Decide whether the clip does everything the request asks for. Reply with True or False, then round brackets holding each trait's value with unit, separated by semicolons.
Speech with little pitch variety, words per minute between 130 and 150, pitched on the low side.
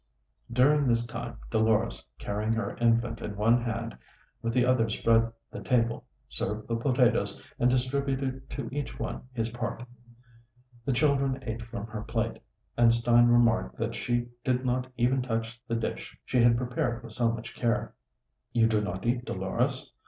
False (1.7 semitones; 165 wpm; 120 Hz)